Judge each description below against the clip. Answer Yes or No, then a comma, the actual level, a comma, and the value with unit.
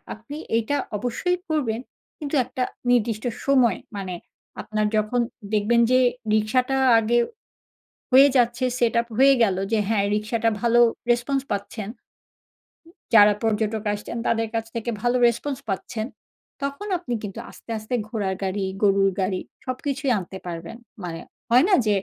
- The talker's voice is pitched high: Yes, high, 230 Hz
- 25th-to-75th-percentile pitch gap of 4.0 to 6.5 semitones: No, average, 3.3 semitones